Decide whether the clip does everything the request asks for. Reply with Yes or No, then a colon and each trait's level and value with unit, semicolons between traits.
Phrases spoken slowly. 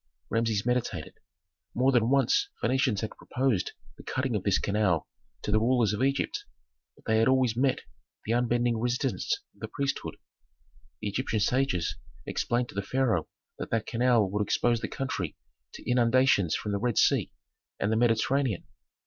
No: average, 165 wpm